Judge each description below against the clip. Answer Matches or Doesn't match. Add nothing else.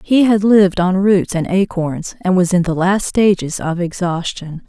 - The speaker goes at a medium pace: Matches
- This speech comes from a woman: Matches